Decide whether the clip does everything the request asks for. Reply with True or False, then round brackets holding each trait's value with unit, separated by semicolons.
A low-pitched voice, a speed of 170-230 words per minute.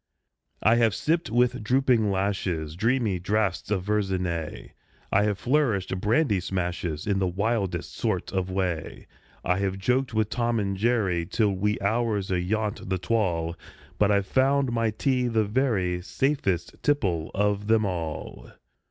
False (100 Hz; 145 wpm)